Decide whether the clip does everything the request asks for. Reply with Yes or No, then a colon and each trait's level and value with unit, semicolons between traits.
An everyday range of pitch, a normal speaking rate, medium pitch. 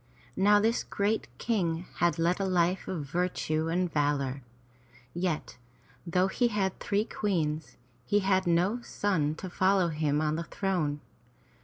Yes: average, 3.8 semitones; average, 150 wpm; medium, 175 Hz